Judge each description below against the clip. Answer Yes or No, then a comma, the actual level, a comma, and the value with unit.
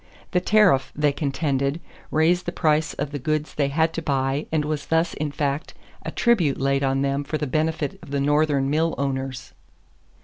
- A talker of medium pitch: Yes, medium, 145 Hz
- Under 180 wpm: No, average, 190 wpm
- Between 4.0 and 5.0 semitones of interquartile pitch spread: No, narrow, 2.4 semitones